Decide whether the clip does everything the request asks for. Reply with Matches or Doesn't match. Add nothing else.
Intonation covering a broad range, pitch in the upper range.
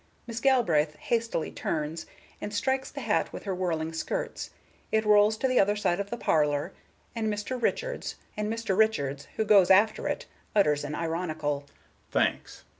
Matches